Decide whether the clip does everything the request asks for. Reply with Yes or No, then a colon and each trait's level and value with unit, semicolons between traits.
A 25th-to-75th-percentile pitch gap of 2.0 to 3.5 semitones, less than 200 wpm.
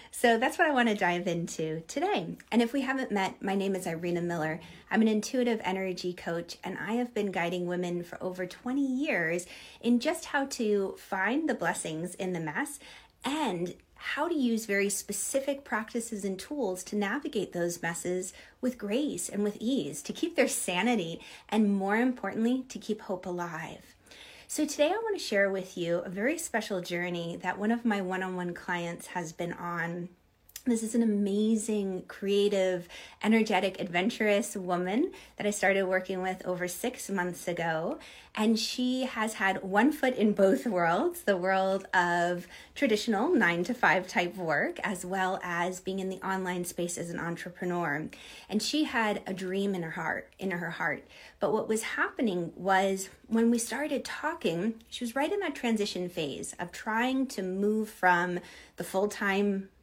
No: average, 4.7 semitones; average, 175 wpm